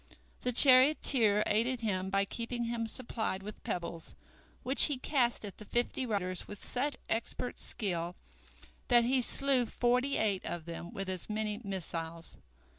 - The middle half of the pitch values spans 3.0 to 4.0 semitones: No, average, 4.6 semitones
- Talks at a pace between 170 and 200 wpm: No, average, 150 wpm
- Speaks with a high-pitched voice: Yes, high, 220 Hz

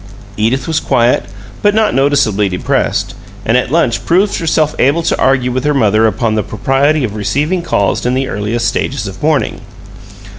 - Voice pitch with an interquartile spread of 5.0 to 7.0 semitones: Yes, wide, 5.4 semitones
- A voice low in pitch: Yes, low, 130 Hz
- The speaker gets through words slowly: No, average, 175 wpm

